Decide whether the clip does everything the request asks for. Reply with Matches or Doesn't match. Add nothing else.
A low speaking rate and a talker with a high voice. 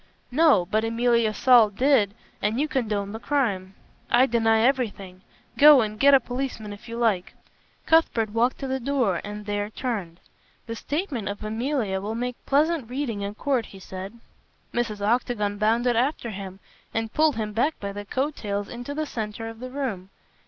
Doesn't match